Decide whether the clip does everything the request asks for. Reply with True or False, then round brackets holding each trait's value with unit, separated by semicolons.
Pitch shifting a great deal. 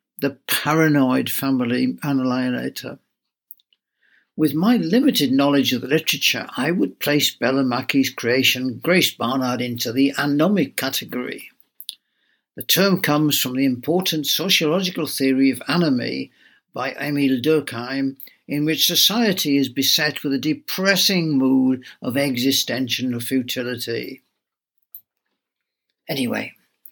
False (3.2 semitones)